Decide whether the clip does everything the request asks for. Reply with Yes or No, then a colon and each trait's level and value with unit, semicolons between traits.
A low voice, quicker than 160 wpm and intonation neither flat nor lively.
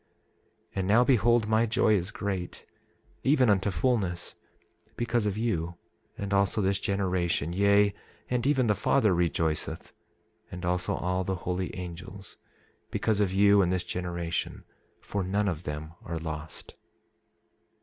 No: very low, 95 Hz; average, 140 wpm; average, 3.1 semitones